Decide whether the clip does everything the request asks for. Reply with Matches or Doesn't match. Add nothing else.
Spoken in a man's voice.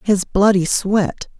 Doesn't match